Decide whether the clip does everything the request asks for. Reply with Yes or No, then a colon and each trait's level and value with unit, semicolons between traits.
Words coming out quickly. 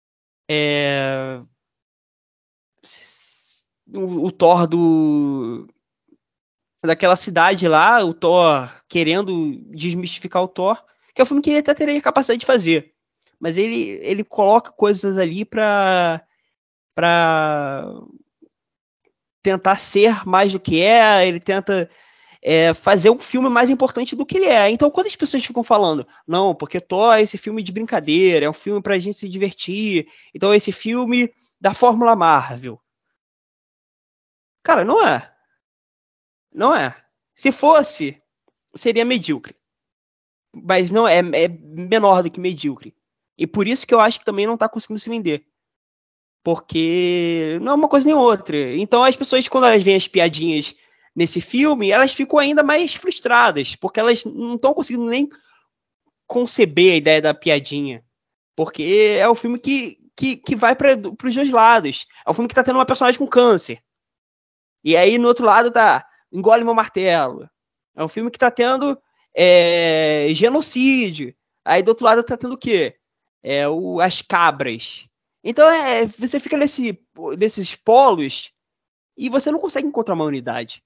No: average, 155 wpm